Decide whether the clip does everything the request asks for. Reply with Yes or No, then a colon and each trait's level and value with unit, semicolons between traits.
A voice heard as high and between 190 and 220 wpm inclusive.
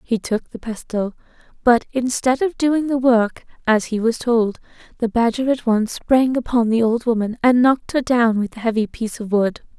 Yes: high, 235 Hz; average, 200 wpm